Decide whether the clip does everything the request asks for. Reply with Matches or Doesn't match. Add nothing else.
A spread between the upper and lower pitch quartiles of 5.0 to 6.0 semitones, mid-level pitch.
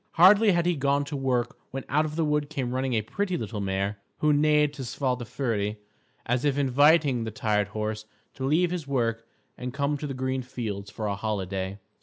Doesn't match